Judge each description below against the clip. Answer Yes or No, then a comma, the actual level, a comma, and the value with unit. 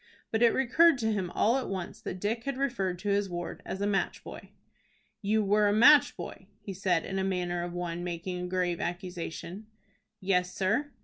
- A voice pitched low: No, high, 195 Hz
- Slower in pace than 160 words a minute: No, average, 200 wpm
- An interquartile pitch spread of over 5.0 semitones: No, average, 3.6 semitones